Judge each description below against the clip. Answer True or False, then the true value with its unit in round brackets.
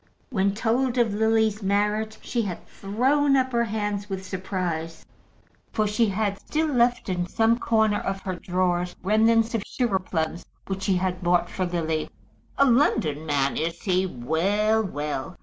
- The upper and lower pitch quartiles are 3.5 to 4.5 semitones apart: True (3.9 semitones)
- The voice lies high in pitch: True (200 Hz)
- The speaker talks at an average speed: True (160 wpm)